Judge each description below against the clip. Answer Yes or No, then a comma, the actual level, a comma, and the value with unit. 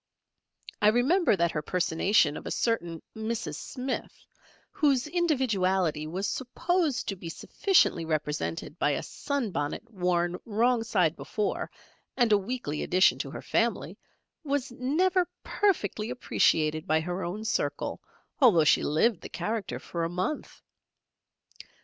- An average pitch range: No, wide, 7.0 semitones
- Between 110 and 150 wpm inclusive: Yes, slow, 135 wpm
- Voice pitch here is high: Yes, high, 205 Hz